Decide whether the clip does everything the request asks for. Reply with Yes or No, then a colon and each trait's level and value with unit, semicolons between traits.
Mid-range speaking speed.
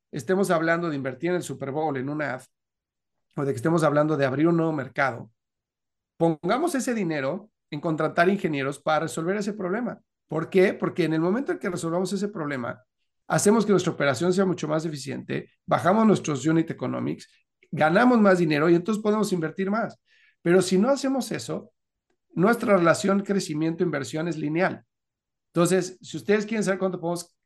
Yes: average, 175 wpm